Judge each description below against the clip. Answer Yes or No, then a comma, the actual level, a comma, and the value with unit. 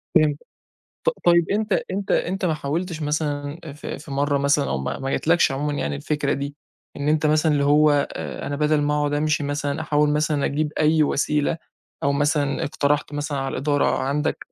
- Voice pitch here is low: No, medium, 150 Hz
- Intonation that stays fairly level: Yes, narrow, 1.3 semitones